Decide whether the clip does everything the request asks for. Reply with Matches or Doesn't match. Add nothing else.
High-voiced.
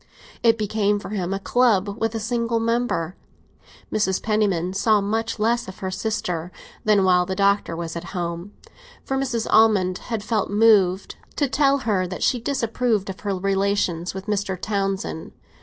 Matches